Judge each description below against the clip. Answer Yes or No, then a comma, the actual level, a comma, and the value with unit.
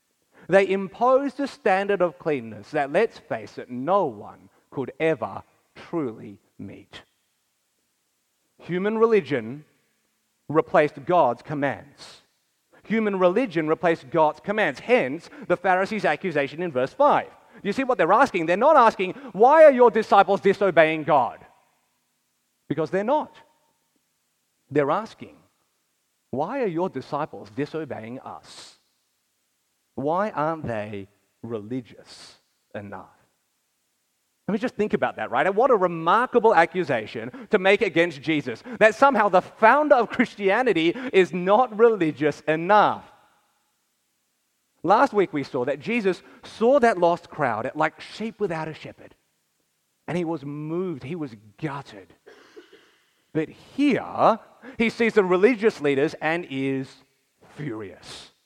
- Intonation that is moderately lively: No, wide, 6.7 semitones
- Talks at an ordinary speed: No, slow, 125 wpm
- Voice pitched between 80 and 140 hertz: No, medium, 180 Hz